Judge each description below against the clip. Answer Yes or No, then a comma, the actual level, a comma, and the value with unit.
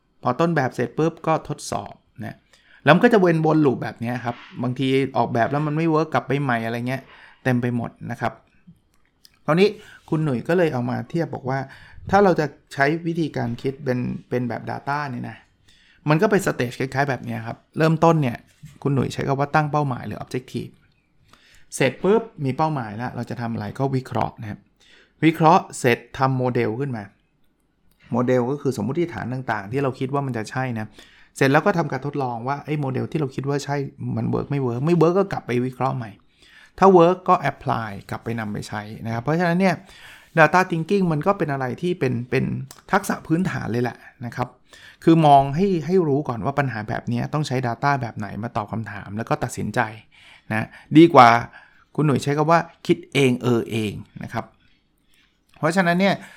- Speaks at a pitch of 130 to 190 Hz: Yes, low, 135 Hz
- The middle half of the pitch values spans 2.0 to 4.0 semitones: No, average, 4.7 semitones